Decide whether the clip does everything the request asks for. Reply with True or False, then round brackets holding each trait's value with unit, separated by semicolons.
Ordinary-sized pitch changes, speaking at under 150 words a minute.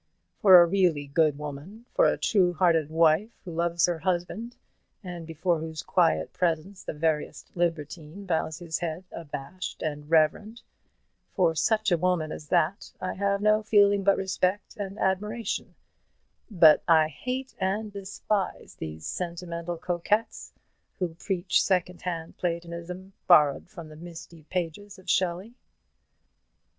True (3.2 semitones; 135 wpm)